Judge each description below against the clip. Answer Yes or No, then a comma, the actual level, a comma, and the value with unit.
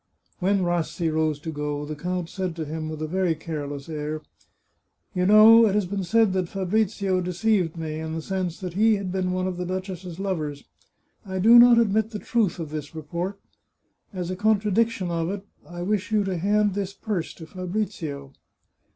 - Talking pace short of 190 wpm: No, average, 195 wpm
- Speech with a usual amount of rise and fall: Yes, average, 3.8 semitones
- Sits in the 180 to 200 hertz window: Yes, medium, 185 Hz